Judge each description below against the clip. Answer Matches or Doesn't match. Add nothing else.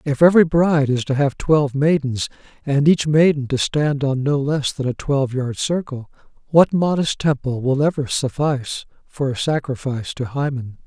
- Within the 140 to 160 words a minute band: Doesn't match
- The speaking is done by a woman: Doesn't match